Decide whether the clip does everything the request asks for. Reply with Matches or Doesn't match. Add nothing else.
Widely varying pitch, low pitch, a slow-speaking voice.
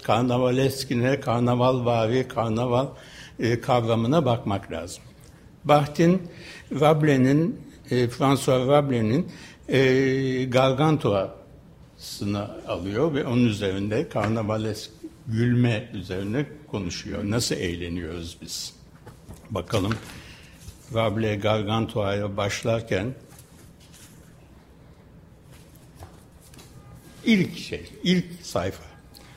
Doesn't match